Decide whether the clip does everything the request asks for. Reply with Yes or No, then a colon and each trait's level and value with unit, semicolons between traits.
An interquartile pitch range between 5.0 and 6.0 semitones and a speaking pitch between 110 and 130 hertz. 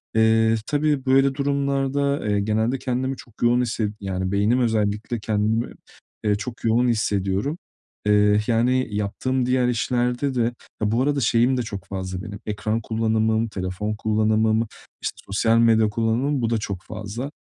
No: average, 3.2 semitones; low, 115 Hz